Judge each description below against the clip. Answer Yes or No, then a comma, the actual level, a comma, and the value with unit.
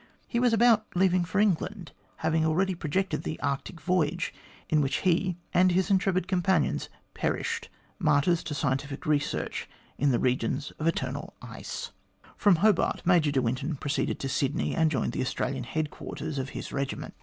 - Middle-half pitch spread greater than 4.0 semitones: Yes, average, 4.7 semitones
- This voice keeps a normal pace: Yes, average, 155 wpm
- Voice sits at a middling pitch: Yes, medium, 160 Hz